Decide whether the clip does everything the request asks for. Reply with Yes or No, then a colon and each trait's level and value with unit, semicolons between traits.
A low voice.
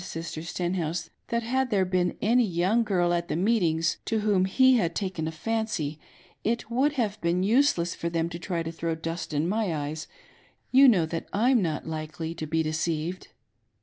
No: medium, 175 Hz